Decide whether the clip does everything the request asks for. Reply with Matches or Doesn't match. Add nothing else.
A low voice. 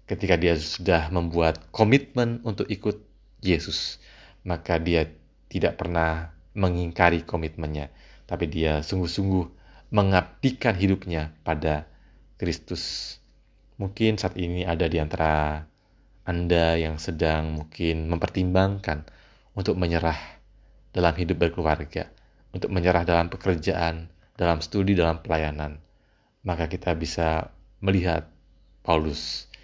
Matches